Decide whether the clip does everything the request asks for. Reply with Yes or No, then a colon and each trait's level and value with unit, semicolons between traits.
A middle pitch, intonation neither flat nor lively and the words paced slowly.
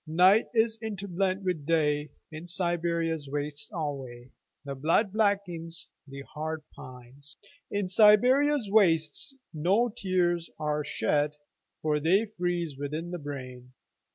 Yes: medium, 165 Hz; average, 4.8 semitones; slow, 100 wpm